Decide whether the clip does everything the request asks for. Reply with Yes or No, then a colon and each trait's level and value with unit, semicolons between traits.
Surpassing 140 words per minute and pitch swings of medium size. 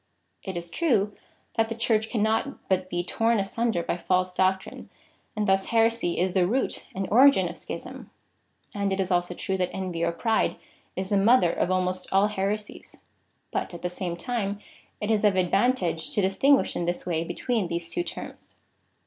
Yes: average, 190 wpm; average, 3.7 semitones